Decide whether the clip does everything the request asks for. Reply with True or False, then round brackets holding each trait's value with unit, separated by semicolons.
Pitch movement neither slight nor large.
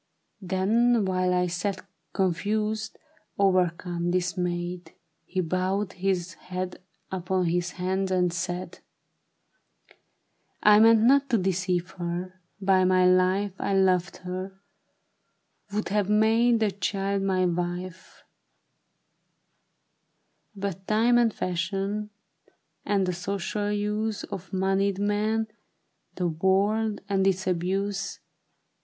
False (2.2 semitones)